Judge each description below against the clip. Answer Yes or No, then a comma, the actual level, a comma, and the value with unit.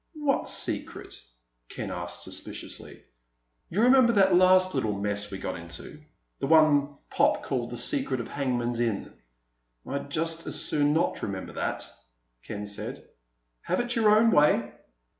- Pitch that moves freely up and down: Yes, wide, 8.6 semitones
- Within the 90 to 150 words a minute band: Yes, average, 140 wpm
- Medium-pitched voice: Yes, medium, 145 Hz